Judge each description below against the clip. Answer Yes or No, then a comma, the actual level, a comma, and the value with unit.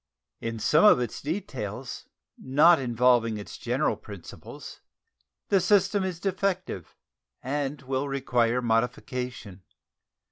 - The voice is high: No, low, 125 Hz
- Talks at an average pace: No, slow, 105 wpm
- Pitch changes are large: No, average, 5.0 semitones